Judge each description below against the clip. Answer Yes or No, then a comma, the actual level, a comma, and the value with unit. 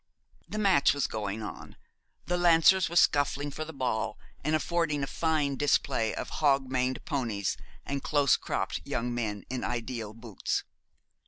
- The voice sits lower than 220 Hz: Yes, medium, 140 Hz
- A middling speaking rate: Yes, average, 155 wpm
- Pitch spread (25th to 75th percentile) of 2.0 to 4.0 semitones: No, average, 4.7 semitones